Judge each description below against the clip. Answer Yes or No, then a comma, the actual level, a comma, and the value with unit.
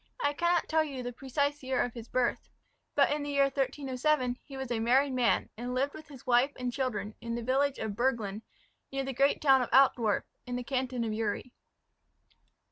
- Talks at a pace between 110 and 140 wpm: No, fast, 205 wpm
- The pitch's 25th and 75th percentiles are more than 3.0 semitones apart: No, narrow, 2.5 semitones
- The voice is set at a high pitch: Yes, very high, 260 Hz